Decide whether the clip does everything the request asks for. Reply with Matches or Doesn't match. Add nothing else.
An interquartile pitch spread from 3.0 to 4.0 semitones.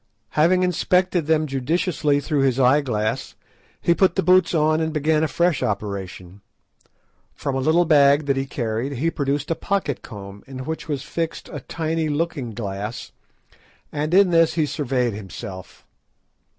Doesn't match